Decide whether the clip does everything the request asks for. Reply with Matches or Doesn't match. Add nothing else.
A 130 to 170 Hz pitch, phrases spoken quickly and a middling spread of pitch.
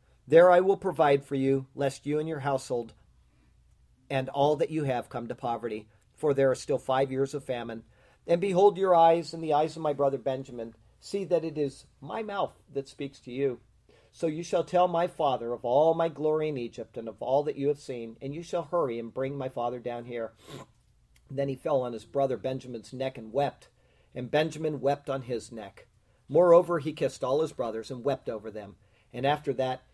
Matches